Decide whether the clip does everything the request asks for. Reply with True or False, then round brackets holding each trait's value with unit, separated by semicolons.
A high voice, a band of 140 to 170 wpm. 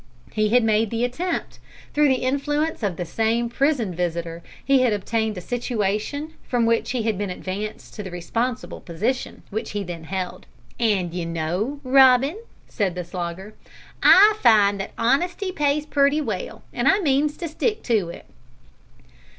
True (230 Hz; 165 wpm)